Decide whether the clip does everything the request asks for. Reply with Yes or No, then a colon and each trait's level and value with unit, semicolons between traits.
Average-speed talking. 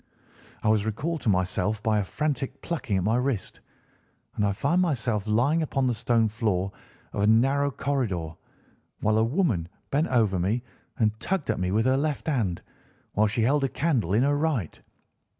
Yes: average, 185 wpm